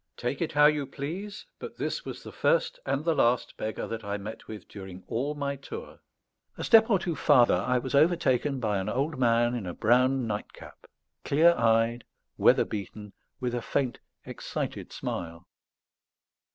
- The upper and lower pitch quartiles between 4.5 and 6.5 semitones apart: Yes, average, 4.9 semitones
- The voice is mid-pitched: No, low, 125 Hz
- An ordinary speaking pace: Yes, average, 170 wpm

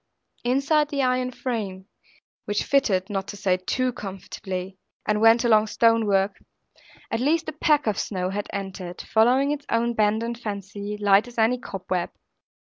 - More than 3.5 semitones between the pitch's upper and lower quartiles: Yes, average, 4.3 semitones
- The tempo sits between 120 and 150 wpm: No, average, 160 wpm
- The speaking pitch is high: Yes, high, 220 Hz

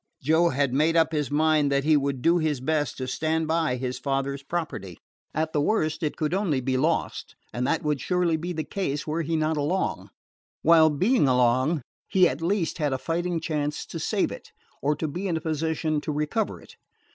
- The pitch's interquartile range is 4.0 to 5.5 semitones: No, average, 2.8 semitones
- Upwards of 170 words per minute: Yes, fast, 205 wpm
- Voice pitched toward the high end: No, medium, 155 Hz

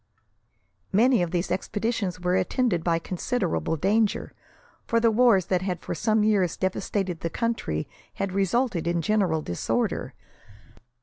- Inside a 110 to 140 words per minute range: Yes, slow, 135 wpm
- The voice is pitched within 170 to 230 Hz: Yes, high, 190 Hz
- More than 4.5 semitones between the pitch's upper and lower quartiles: No, average, 4.2 semitones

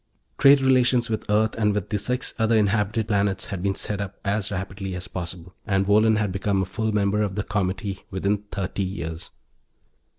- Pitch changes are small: Yes, narrow, 2.0 semitones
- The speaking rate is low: No, average, 190 wpm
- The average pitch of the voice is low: Yes, low, 100 Hz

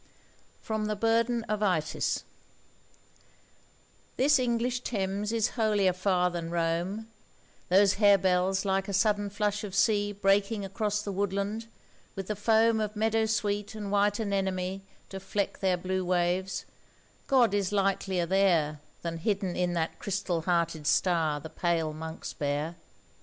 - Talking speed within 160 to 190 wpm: No, slow, 135 wpm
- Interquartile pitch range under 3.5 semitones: Yes, average, 2.7 semitones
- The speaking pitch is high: Yes, high, 195 Hz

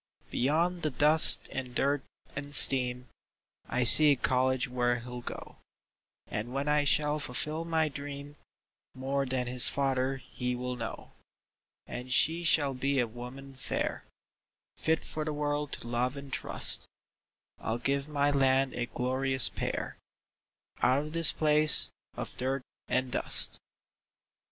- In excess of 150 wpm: No, average, 140 wpm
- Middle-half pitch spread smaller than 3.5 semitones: Yes, average, 2.7 semitones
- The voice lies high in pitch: No, low, 135 Hz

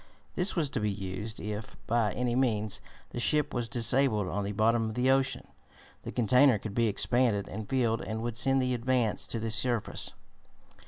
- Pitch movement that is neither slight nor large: Yes, average, 3.0 semitones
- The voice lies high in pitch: No, low, 115 Hz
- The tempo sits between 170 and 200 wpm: Yes, average, 190 wpm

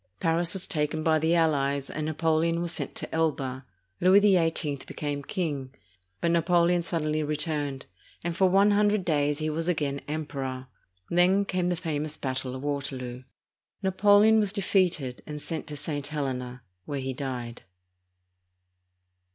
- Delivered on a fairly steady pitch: No, average, 3.7 semitones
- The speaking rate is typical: Yes, average, 145 wpm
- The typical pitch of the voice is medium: Yes, medium, 155 Hz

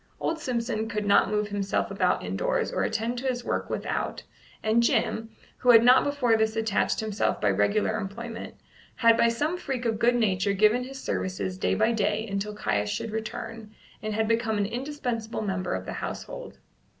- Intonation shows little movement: Yes, narrow, 2.3 semitones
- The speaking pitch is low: No, high, 220 Hz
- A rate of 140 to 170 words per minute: No, average, 185 wpm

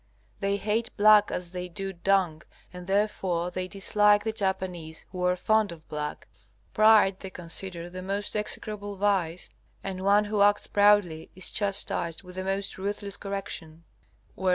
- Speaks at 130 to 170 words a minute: Yes, average, 155 wpm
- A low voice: No, high, 195 Hz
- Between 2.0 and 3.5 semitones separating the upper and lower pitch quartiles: Yes, narrow, 2.4 semitones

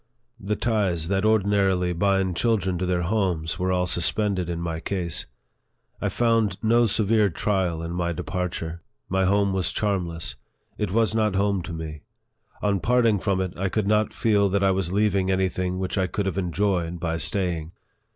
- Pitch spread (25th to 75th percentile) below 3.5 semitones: Yes, average, 2.8 semitones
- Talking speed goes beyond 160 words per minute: Yes, average, 180 wpm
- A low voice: Yes, very low, 95 Hz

